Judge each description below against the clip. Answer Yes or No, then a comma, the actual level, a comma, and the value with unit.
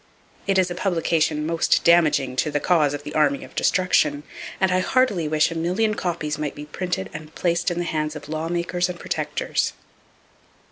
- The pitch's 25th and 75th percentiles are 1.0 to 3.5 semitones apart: Yes, average, 2.9 semitones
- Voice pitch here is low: No, medium, 165 Hz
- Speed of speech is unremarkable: Yes, average, 185 wpm